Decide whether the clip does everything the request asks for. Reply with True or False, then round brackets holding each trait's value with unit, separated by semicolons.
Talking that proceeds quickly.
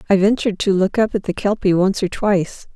True (240 wpm)